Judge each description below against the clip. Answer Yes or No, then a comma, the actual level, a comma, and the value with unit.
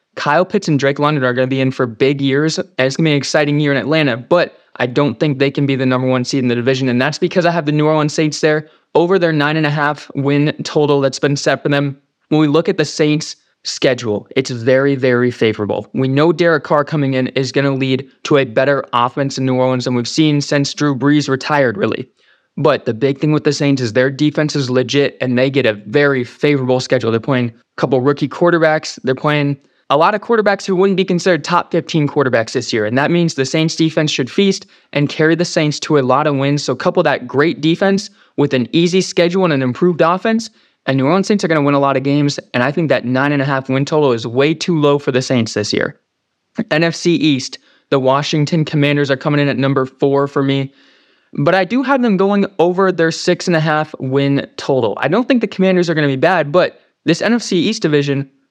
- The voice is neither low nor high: Yes, medium, 145 Hz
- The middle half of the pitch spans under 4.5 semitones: Yes, average, 3.3 semitones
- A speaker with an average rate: No, fast, 245 wpm